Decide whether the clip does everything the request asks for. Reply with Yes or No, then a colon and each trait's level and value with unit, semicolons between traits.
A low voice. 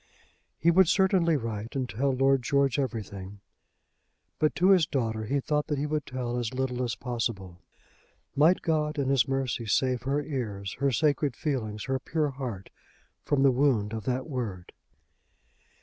Yes: low, 130 Hz